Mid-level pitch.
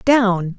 No: high, 210 Hz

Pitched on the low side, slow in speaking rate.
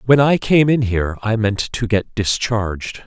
No: low, 110 Hz; average, 195 wpm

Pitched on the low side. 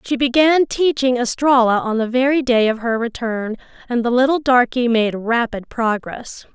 No: high, 245 Hz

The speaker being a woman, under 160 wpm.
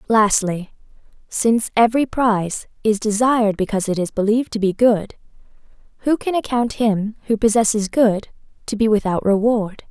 Yes: female; average, 145 wpm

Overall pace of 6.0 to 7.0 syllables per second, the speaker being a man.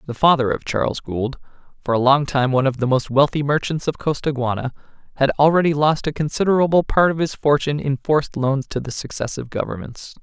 Yes: 6.1 syllables/s; male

